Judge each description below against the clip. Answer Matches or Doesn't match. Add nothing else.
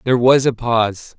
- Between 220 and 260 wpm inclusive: Doesn't match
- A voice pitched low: Matches